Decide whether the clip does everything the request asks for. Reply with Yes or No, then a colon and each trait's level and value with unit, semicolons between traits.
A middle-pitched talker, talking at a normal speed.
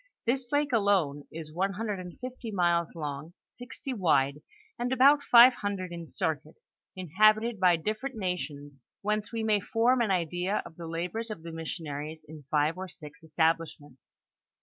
Yes: medium, 180 Hz; average, 165 wpm